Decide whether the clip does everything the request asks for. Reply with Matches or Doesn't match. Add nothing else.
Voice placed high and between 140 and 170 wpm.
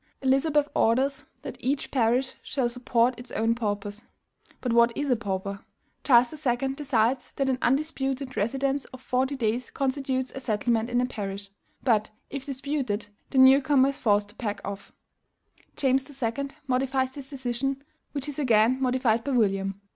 Matches